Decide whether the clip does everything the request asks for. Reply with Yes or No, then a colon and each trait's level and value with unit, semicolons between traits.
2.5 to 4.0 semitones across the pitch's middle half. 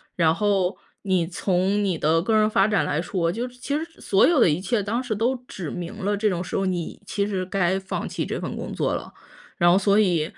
Yes: average, 3.2 semitones